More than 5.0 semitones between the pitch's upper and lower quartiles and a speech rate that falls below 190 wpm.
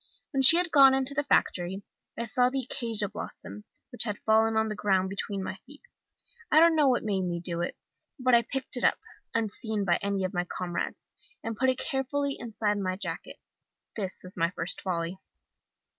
No: wide, 5.5 semitones; average, 195 wpm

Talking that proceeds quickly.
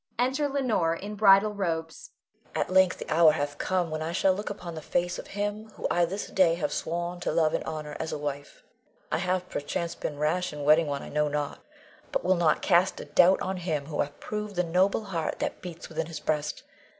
Yes: fast, 225 wpm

